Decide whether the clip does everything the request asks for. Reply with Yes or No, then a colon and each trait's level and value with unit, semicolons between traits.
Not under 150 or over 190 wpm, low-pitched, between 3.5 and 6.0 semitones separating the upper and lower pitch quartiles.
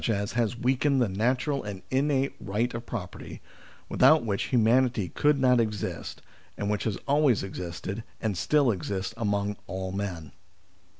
No: average, 140 wpm; low, 110 Hz; average, 4.5 semitones